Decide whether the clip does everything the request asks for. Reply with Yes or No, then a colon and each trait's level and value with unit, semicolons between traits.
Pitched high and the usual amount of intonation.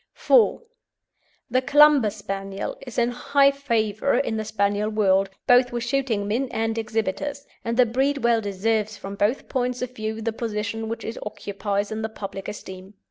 Yes: high, 225 Hz; average, 3.3 semitones